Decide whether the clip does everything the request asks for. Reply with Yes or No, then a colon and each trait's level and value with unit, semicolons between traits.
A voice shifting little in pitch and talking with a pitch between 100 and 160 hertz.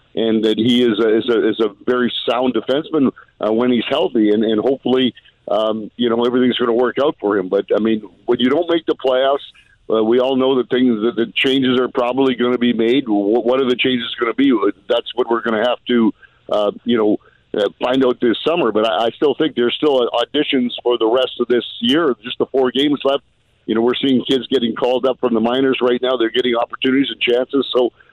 Yes: narrow, 2.1 semitones; low, 125 Hz